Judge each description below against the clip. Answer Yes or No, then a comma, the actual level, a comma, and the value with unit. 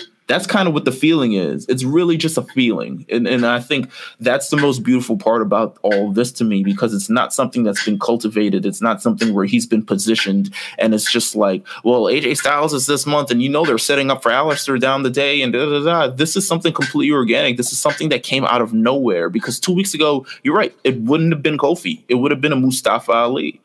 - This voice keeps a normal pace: No, fast, 245 wpm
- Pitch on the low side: Yes, low, 130 Hz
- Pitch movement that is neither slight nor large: Yes, average, 4.8 semitones